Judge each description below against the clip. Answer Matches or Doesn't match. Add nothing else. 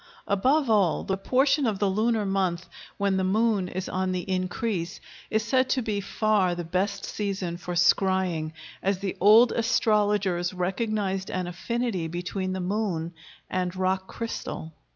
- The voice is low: Doesn't match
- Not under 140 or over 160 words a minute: Matches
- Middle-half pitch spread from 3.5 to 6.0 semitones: Doesn't match